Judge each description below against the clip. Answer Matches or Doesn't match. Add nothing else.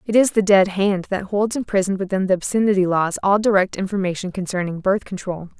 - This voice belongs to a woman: Matches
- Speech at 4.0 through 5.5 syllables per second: Doesn't match